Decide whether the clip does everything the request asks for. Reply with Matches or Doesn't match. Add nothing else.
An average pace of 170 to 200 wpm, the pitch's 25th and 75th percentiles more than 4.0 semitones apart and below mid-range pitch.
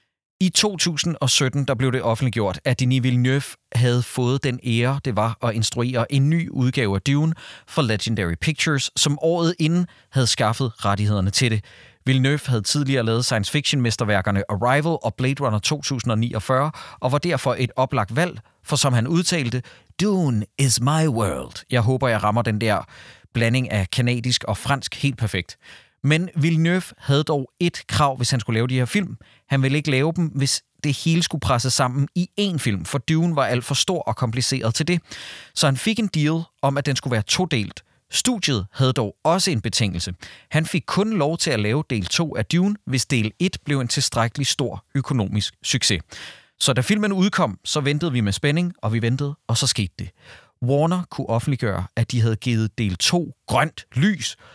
Matches